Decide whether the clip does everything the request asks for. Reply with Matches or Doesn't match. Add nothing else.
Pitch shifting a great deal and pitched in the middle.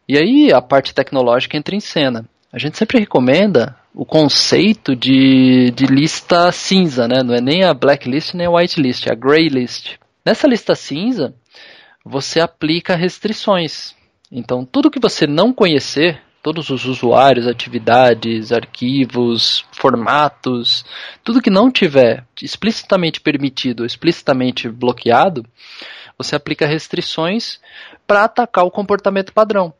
Matches